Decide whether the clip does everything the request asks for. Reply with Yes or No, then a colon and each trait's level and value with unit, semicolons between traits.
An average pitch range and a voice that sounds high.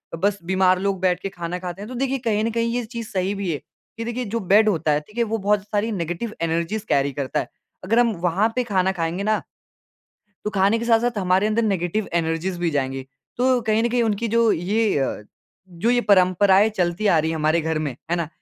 Yes: average, 4.5 semitones; high, 195 Hz